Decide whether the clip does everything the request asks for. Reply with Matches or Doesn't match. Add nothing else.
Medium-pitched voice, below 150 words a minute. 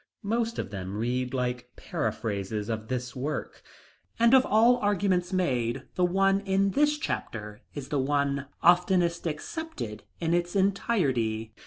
Matches